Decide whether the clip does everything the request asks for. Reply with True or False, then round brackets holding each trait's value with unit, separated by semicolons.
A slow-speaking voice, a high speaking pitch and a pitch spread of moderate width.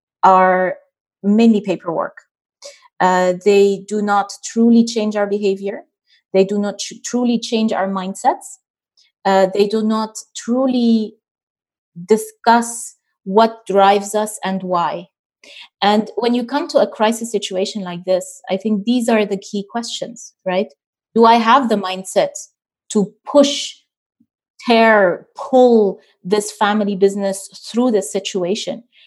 True (130 wpm; 210 Hz; 3.0 semitones)